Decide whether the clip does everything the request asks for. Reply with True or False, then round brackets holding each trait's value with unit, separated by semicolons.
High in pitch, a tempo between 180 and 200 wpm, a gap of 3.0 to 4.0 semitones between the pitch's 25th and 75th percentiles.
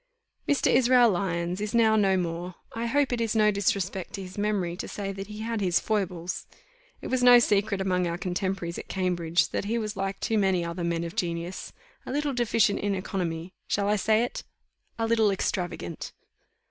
True (195 Hz; 195 wpm; 3.6 semitones)